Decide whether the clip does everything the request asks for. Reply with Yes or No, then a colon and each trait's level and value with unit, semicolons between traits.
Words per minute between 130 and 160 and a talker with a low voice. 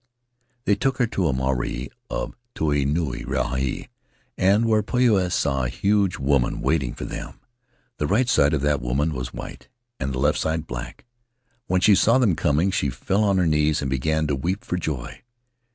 No: average, 185 wpm; very low, 75 Hz